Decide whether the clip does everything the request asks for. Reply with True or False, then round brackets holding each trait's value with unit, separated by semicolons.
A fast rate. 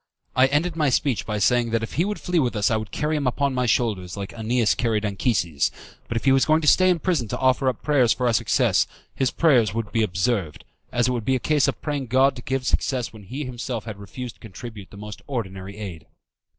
True (245 wpm)